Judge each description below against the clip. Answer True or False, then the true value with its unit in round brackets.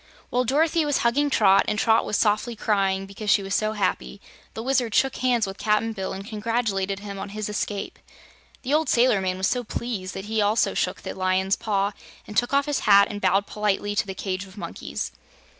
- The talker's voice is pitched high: True (210 Hz)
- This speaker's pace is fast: True (210 wpm)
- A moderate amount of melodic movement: True (3.2 semitones)